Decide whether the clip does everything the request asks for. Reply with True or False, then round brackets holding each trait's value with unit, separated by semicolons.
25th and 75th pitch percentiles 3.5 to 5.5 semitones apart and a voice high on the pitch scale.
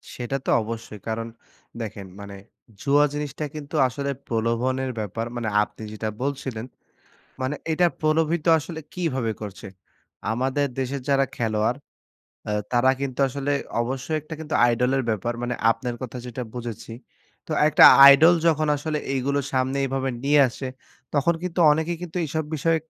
False (4.1 semitones; 130 Hz)